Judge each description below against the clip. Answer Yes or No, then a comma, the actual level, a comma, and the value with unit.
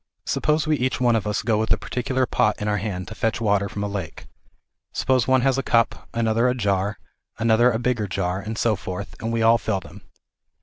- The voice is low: Yes, low, 110 Hz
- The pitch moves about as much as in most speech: Yes, average, 3.1 semitones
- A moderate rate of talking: No, fast, 225 wpm